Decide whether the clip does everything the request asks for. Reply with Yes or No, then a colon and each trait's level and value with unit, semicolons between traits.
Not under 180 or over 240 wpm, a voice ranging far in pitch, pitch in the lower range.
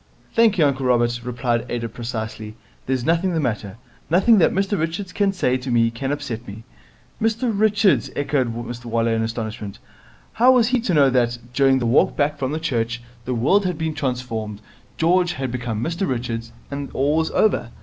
Yes: average, 185 wpm; wide, 6.3 semitones; low, 130 Hz